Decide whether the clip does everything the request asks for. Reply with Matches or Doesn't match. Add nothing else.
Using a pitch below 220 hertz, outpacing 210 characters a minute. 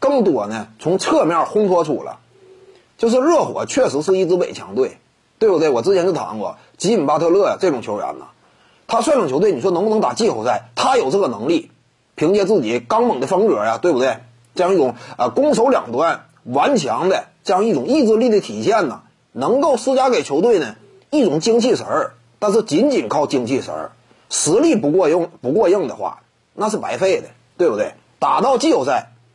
Doesn't match